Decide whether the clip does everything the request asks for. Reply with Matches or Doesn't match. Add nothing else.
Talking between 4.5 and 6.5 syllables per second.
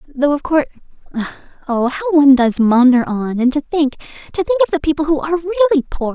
Doesn't match